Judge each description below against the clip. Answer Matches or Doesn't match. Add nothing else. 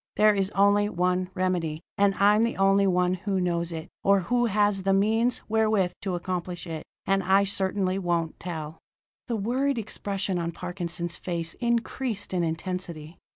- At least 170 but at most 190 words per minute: Doesn't match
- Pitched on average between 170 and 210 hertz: Matches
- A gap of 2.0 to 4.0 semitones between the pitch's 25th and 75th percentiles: Matches